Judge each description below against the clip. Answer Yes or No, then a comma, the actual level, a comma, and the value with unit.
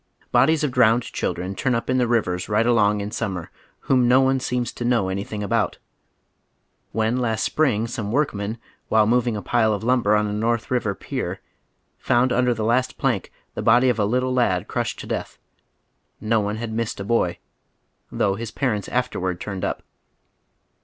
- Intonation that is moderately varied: Yes, average, 3.1 semitones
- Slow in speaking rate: No, average, 180 wpm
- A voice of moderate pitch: No, low, 115 Hz